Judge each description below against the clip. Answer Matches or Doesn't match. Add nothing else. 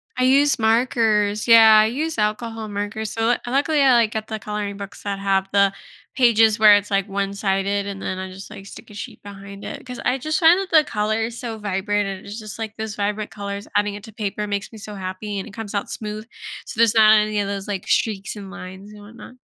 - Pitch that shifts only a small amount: Matches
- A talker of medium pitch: Doesn't match